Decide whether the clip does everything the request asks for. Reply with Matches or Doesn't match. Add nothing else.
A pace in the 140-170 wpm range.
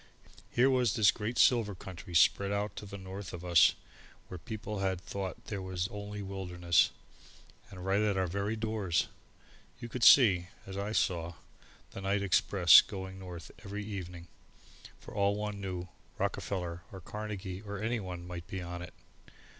Matches